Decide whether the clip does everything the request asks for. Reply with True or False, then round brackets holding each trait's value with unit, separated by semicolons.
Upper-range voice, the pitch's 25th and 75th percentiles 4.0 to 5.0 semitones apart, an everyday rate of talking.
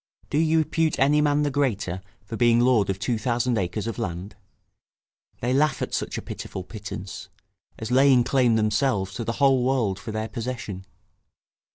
False (120 Hz; 4.5 semitones; 175 wpm)